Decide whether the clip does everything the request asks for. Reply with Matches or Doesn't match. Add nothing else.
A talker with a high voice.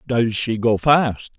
Doesn't match